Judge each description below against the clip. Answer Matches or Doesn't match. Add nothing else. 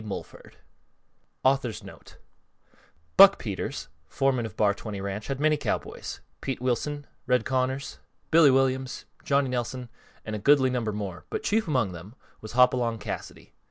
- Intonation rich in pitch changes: Doesn't match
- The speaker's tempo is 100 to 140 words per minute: Matches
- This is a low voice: Matches